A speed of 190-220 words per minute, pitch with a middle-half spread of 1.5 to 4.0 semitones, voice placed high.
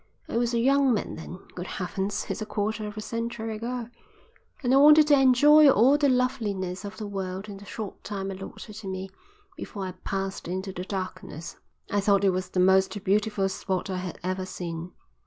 Yes: average, 200 wpm; average, 3.6 semitones; high, 200 Hz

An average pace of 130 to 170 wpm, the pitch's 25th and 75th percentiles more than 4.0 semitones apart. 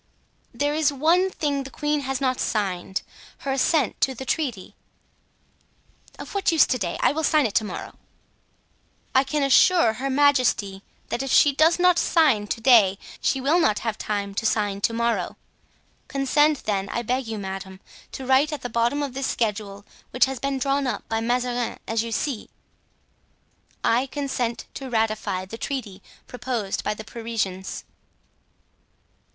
Yes: average, 165 wpm; average, 4.5 semitones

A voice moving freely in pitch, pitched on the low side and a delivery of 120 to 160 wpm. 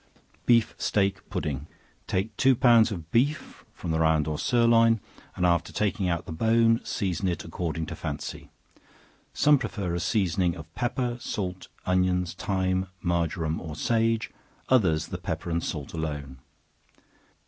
Yes: wide, 5.7 semitones; very low, 90 Hz; average, 145 wpm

